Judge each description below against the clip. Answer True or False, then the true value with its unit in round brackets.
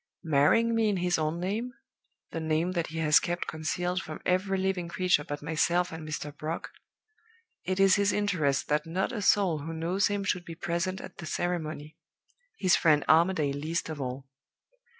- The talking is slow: False (180 wpm)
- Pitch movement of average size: True (3.3 semitones)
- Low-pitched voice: False (170 Hz)